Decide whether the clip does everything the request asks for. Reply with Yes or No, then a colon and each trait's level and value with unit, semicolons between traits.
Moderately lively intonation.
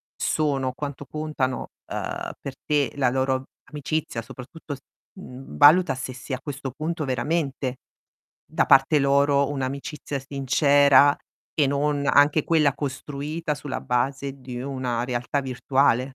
No: narrow, 1.9 semitones